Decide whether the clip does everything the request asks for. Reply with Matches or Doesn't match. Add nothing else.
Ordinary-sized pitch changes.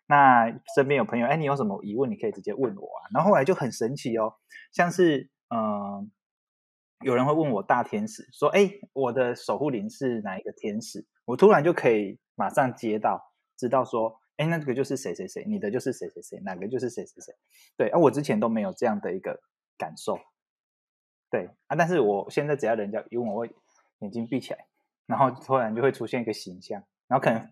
Doesn't match